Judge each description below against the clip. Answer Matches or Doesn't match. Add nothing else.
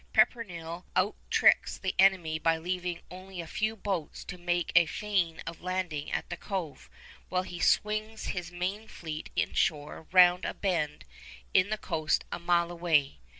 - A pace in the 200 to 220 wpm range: Doesn't match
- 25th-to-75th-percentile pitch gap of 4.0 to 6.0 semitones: Doesn't match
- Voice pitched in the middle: Matches